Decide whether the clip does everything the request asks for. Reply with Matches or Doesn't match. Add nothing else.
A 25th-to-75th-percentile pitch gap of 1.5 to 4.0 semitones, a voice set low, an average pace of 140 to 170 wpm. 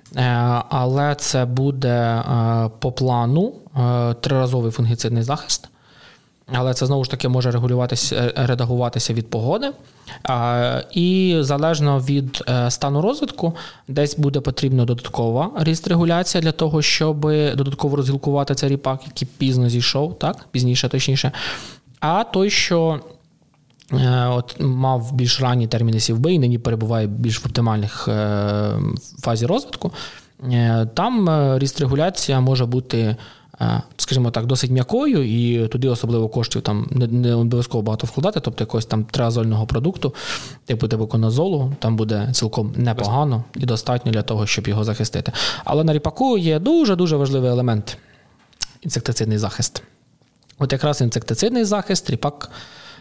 Doesn't match